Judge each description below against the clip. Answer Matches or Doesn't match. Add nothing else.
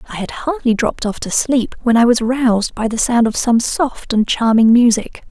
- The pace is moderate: Doesn't match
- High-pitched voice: Matches